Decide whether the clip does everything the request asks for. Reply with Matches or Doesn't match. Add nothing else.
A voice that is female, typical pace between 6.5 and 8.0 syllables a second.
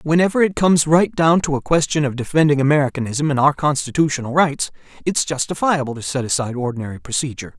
Doesn't match